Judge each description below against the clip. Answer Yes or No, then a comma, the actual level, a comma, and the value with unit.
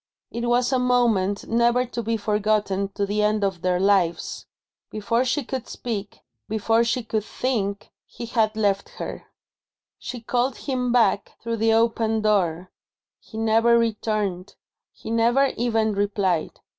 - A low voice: No, high, 220 Hz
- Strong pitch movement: No, narrow, 2.6 semitones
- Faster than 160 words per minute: No, average, 145 wpm